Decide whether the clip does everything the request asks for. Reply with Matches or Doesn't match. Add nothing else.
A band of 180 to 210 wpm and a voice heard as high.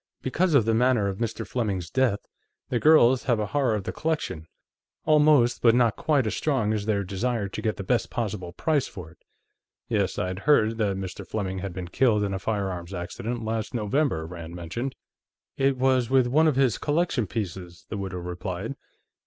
Doesn't match